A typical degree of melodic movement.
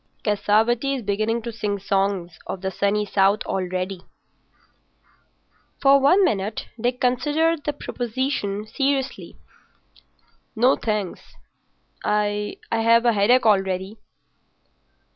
Yes: average, 3.9 semitones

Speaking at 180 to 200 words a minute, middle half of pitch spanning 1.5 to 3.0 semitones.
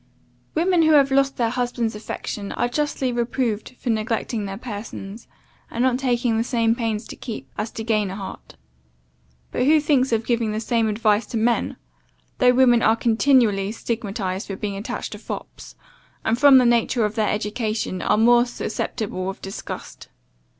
No: average, 170 wpm; average, 2.7 semitones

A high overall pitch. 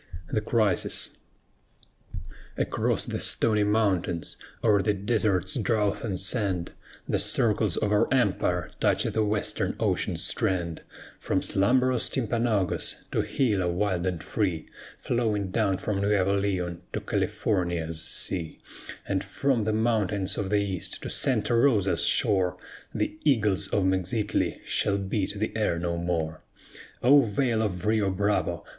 No: low, 100 Hz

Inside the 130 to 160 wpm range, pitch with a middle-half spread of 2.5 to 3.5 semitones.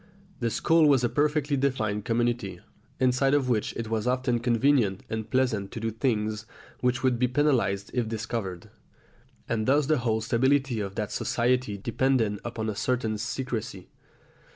Yes: average, 155 wpm; average, 3.2 semitones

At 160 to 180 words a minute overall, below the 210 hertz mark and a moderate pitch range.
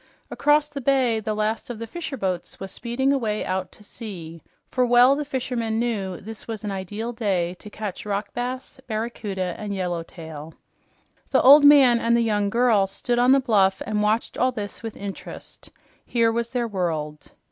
No: average, 175 wpm; high, 220 Hz; average, 3.9 semitones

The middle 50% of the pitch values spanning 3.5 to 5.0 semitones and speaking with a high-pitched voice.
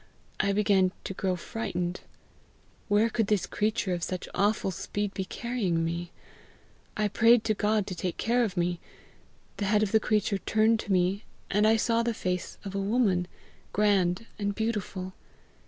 No: average, 2.9 semitones; high, 205 Hz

